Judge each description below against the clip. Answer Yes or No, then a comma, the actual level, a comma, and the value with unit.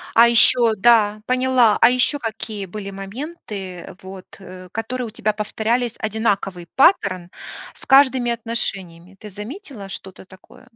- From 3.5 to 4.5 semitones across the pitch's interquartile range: Yes, average, 3.9 semitones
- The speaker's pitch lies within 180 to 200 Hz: No, high, 215 Hz